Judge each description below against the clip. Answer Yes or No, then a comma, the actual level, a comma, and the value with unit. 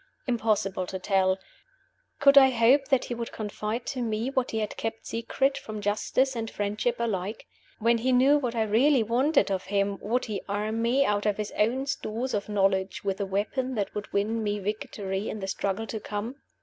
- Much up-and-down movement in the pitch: No, average, 3.3 semitones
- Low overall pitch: No, high, 220 Hz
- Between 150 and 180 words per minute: No, average, 200 wpm